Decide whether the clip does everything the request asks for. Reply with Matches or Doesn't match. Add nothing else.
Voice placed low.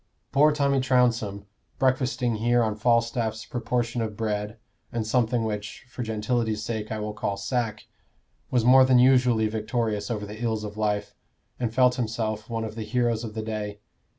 Matches